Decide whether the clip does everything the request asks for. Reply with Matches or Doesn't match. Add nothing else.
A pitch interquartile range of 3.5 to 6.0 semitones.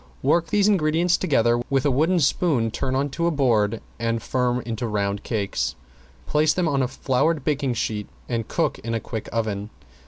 Matches